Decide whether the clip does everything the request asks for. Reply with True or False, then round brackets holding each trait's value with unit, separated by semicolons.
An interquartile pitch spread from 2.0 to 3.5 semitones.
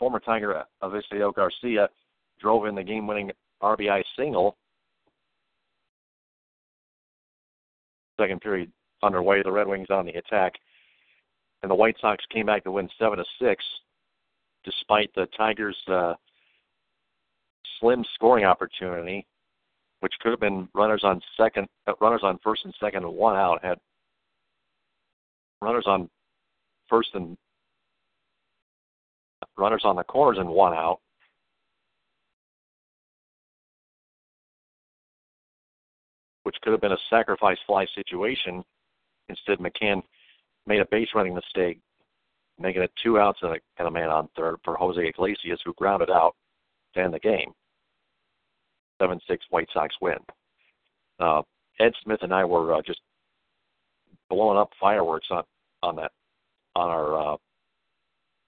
True (2.9 semitones)